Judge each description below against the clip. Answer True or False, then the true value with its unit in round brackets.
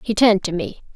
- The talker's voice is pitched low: False (200 Hz)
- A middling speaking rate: False (250 wpm)